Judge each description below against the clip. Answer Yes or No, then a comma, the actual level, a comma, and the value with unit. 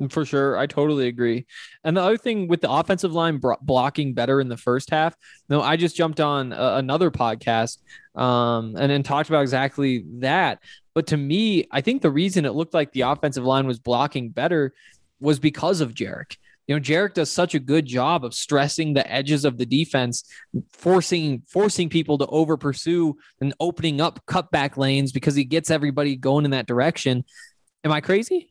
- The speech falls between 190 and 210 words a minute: Yes, average, 200 wpm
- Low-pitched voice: No, medium, 145 Hz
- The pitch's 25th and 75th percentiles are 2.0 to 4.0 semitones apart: Yes, average, 3.4 semitones